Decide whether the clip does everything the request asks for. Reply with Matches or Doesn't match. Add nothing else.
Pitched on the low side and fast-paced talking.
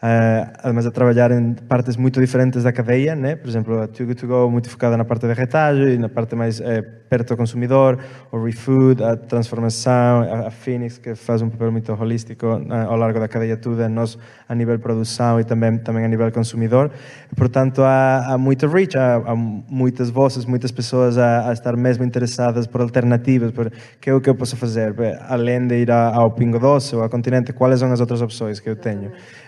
Matches